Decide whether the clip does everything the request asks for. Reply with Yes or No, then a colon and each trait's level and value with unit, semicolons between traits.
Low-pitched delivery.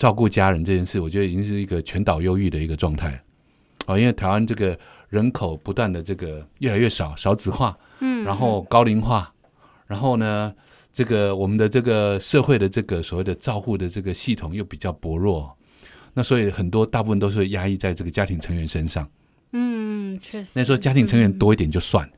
Yes: low, 100 Hz